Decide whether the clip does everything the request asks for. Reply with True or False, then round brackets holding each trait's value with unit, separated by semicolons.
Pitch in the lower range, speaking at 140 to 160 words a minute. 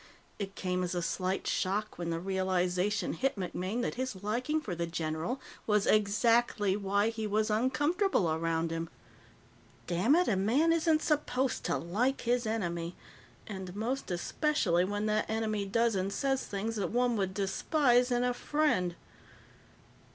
False (210 Hz; 150 wpm)